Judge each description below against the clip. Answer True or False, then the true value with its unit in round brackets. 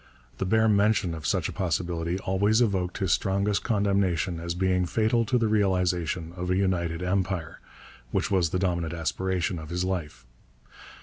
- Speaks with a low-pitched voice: True (95 Hz)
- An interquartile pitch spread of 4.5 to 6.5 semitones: False (2.5 semitones)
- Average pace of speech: True (165 wpm)